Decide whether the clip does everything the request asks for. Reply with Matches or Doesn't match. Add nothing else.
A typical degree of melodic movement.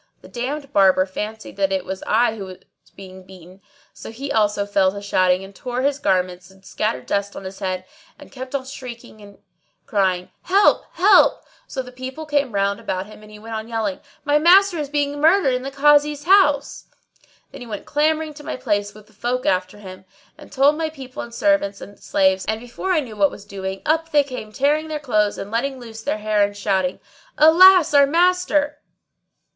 Doesn't match